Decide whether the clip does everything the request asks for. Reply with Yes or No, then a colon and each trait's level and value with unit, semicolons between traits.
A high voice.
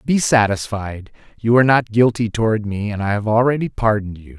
No: low, 110 Hz